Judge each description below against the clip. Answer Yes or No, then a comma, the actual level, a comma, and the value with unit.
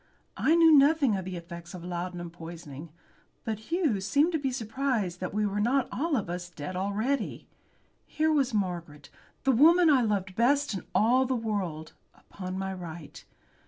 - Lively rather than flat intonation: Yes, wide, 7.3 semitones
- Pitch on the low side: No, high, 205 Hz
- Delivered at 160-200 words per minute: Yes, average, 170 wpm